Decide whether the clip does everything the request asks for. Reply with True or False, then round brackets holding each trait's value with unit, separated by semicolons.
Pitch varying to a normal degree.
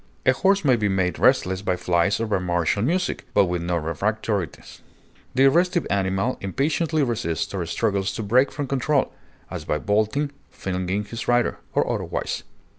False (6.4 semitones)